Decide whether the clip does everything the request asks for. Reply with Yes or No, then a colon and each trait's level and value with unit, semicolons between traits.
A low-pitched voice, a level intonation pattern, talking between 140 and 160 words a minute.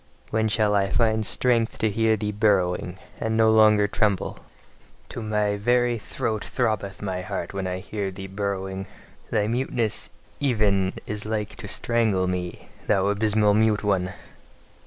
Yes: low, 105 Hz; narrow, 2.2 semitones; average, 150 wpm